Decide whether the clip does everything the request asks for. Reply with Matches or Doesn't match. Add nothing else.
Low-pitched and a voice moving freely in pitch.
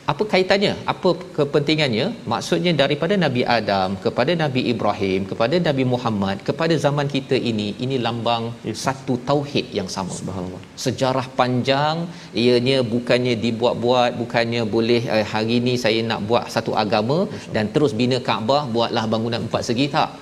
Doesn't match